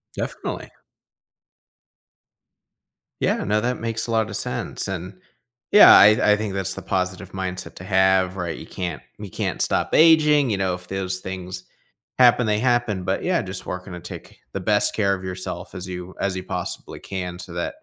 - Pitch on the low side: Yes, very low, 95 Hz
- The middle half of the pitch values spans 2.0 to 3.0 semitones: Yes, average, 2.7 semitones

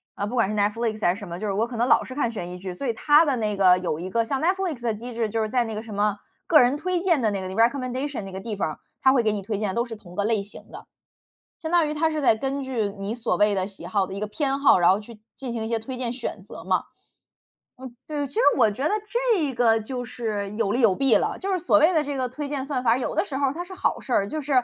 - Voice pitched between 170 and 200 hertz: No, high, 235 Hz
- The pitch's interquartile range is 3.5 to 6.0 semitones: Yes, average, 5.0 semitones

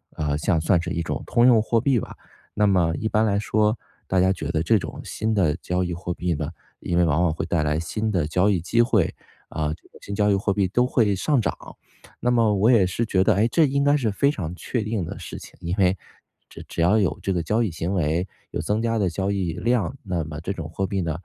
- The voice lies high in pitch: No, very low, 95 Hz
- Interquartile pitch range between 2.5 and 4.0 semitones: No, average, 4.4 semitones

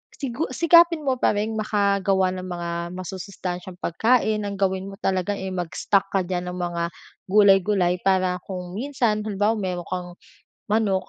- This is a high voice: Yes, high, 195 Hz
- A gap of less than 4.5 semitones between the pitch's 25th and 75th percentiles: Yes, average, 2.7 semitones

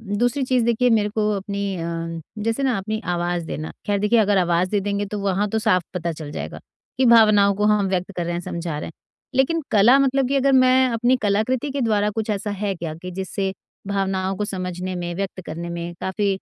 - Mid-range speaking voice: No, high, 200 Hz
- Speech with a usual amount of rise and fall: Yes, average, 3.7 semitones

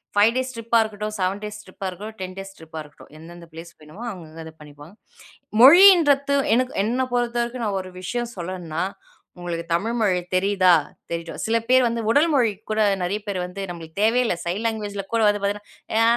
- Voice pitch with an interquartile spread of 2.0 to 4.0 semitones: No, average, 4.8 semitones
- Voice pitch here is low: No, high, 205 Hz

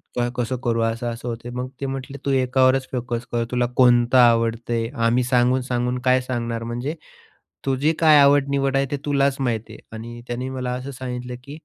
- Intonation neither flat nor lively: No, narrow, 2.0 semitones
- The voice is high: No, low, 125 Hz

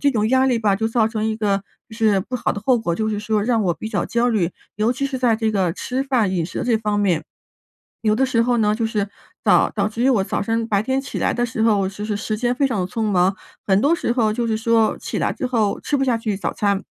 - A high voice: Yes, high, 220 Hz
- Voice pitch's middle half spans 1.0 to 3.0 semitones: Yes, average, 2.7 semitones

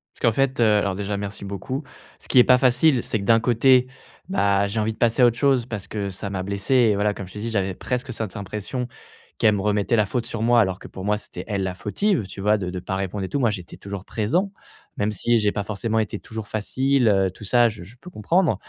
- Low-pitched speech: Yes, low, 105 Hz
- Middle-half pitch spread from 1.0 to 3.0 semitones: No, average, 3.4 semitones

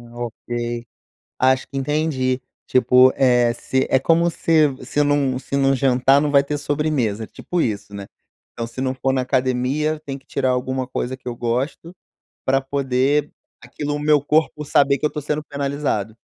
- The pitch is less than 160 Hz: Yes, low, 135 Hz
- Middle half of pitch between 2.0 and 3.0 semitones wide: Yes, narrow, 2.6 semitones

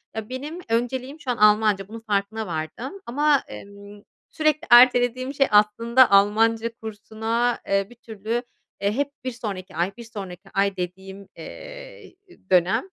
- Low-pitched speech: No, high, 225 Hz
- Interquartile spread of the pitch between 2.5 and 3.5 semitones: No, average, 4.1 semitones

